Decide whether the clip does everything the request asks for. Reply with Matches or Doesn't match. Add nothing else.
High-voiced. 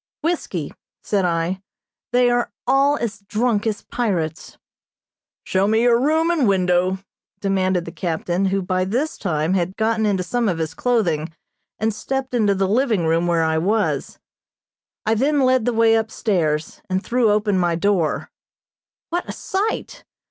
Matches